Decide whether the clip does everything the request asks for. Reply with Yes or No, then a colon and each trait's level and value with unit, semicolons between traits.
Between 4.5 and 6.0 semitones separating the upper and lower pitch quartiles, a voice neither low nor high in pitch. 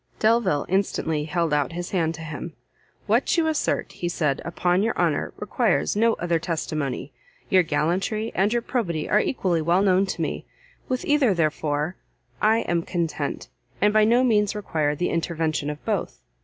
Yes: average, 4.9 semitones; medium, 175 Hz